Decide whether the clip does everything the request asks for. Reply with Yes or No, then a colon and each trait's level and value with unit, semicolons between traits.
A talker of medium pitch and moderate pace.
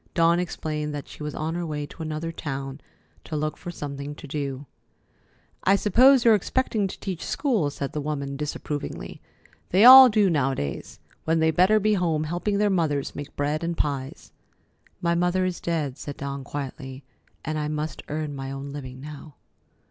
Yes: medium, 155 Hz; average, 180 wpm